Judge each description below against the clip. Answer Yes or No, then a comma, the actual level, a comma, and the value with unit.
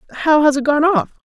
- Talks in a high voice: Yes, very high, 295 Hz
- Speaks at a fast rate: Yes, fast, 240 wpm